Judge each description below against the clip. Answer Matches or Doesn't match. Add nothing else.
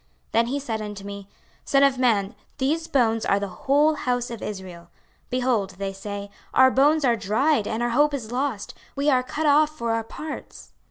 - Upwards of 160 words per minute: Matches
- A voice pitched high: Matches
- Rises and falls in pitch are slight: Doesn't match